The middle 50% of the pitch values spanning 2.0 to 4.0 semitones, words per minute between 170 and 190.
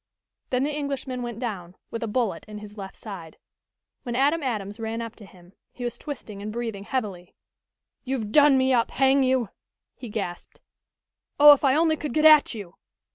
No: average, 4.5 semitones; average, 185 wpm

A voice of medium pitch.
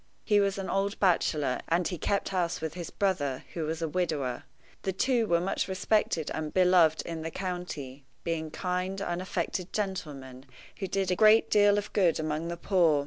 Yes: medium, 175 Hz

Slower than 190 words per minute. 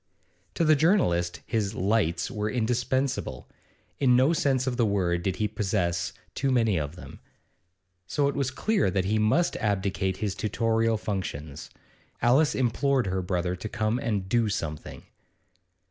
Yes: average, 150 wpm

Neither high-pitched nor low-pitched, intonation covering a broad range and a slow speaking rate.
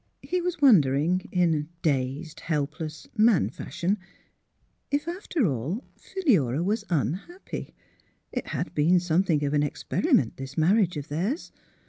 Yes: medium, 170 Hz; wide, 7.1 semitones; slow, 130 wpm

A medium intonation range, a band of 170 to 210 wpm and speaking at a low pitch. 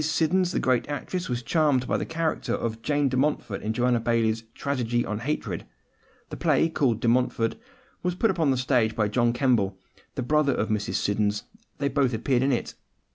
Yes: average, 4.3 semitones; average, 190 wpm; low, 125 Hz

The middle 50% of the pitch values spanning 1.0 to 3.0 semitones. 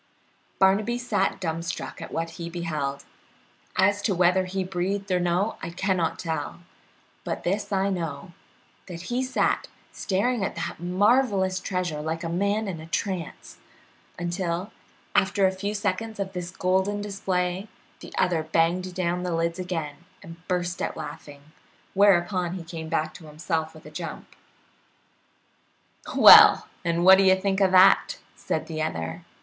Yes: narrow, 2.6 semitones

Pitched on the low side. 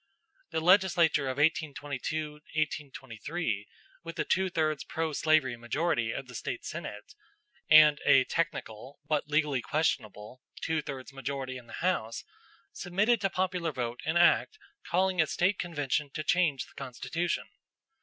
No: medium, 150 Hz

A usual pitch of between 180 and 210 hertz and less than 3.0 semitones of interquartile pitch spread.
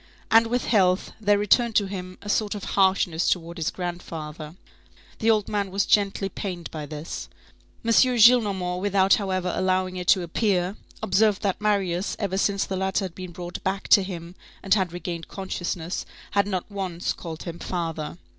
Yes: high, 190 Hz; narrow, 2.5 semitones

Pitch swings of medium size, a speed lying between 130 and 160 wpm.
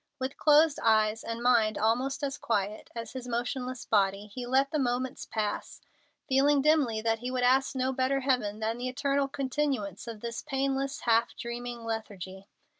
No: average, 3.2 semitones; average, 170 wpm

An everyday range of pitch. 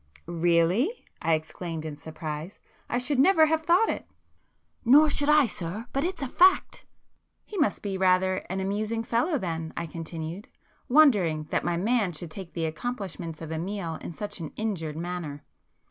No: wide, 7.1 semitones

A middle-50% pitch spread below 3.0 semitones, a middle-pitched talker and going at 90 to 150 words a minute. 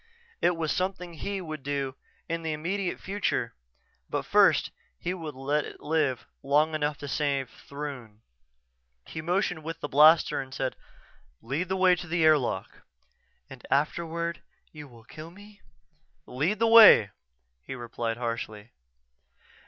No: average, 4.4 semitones; medium, 155 Hz; average, 145 wpm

